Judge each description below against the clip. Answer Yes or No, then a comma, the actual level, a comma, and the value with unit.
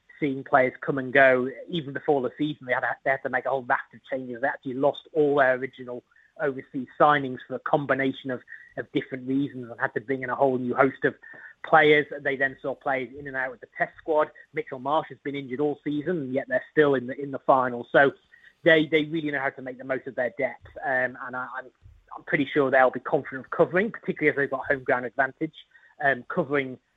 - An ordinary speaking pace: No, fast, 240 wpm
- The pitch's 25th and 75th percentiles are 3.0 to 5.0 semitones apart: No, narrow, 2.4 semitones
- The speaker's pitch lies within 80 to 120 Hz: No, low, 135 Hz